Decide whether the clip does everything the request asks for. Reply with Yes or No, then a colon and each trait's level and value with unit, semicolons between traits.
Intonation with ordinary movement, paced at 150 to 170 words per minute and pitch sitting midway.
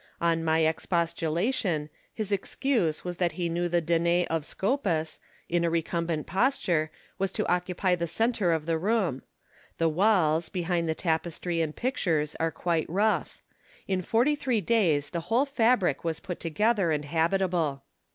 Yes: average, 3.2 semitones; average, 160 wpm; medium, 170 Hz